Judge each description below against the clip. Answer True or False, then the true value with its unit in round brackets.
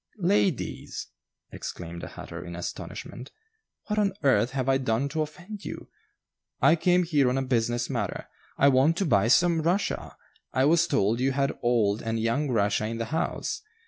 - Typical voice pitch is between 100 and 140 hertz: True (135 Hz)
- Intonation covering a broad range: True (6.1 semitones)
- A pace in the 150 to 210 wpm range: True (175 wpm)